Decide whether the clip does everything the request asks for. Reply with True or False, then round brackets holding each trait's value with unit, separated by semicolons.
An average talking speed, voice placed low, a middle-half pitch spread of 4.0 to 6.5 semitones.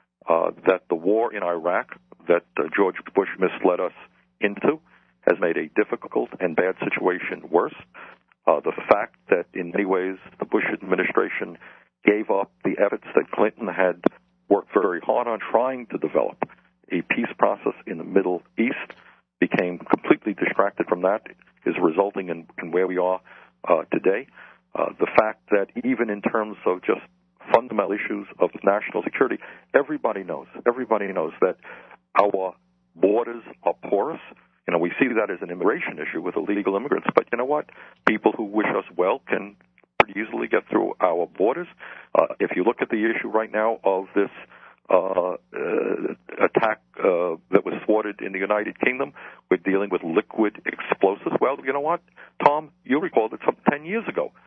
True (170 wpm; 100 Hz; 5.6 semitones)